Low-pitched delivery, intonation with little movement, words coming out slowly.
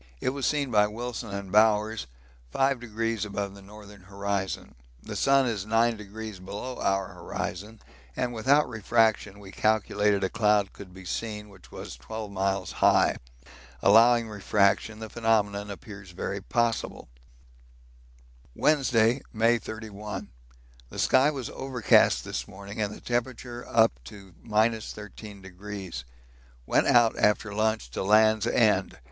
Yes: low, 105 Hz; narrow, 2.3 semitones; slow, 130 wpm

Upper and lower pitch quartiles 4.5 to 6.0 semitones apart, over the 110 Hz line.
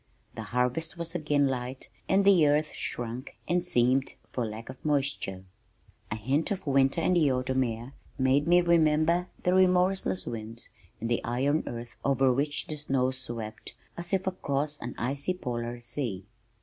Yes: average, 4.8 semitones; low, 135 Hz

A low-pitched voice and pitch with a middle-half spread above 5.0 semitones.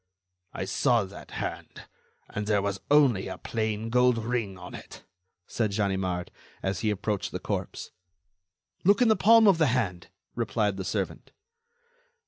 No: low, 110 Hz; average, 4.4 semitones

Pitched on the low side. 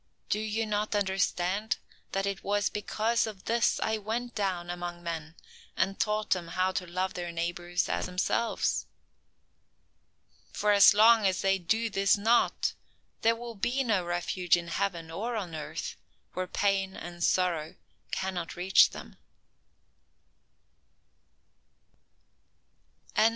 No: high, 195 Hz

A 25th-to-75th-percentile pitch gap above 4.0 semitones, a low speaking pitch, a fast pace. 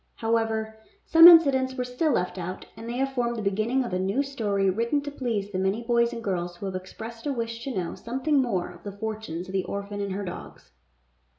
No: average, 4.4 semitones; high, 225 Hz; fast, 225 wpm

